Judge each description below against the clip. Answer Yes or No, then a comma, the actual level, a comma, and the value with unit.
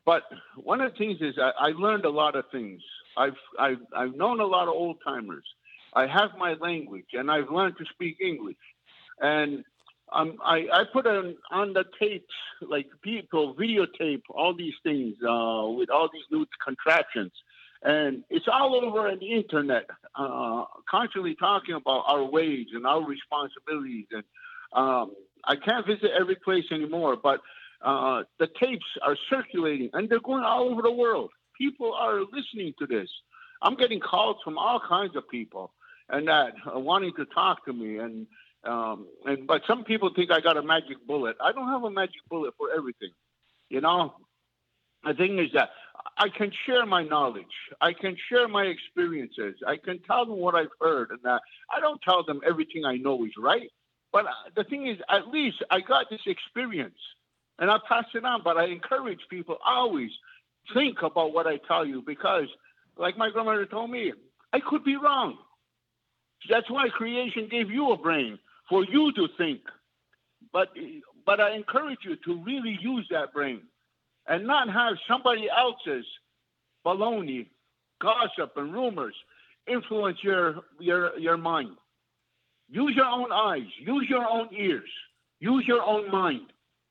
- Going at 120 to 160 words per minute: No, average, 170 wpm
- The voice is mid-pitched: No, high, 200 Hz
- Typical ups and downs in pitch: No, wide, 7.7 semitones